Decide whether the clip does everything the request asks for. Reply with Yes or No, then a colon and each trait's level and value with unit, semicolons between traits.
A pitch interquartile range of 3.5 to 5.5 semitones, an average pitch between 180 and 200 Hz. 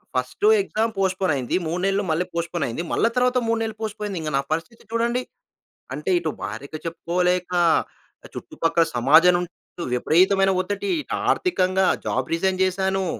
Yes: average, 3.9 semitones; medium, 185 Hz